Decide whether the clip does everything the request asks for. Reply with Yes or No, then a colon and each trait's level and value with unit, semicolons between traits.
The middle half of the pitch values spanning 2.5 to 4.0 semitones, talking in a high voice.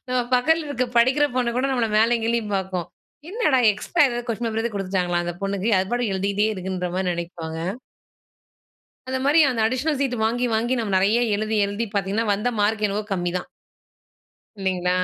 No: average, 4.4 semitones; high, 220 Hz